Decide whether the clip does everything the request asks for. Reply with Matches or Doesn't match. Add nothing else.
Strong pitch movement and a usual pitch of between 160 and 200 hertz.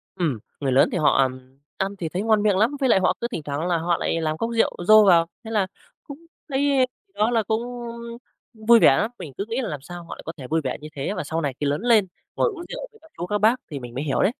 Matches